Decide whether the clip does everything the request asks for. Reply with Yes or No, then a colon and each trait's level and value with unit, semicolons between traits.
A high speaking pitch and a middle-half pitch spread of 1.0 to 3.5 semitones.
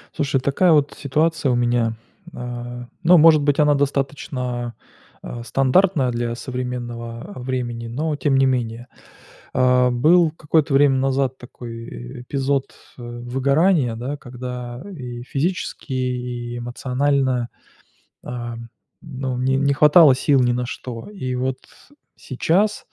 No: low, 130 Hz; average, 2.8 semitones